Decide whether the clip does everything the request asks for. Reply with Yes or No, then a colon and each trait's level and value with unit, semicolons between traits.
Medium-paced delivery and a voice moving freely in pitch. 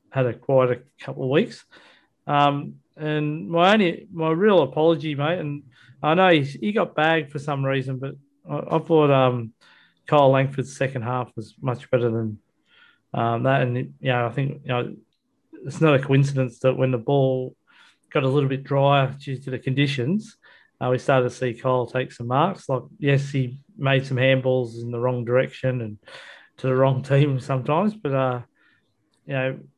No: average, 185 wpm; average, 2.7 semitones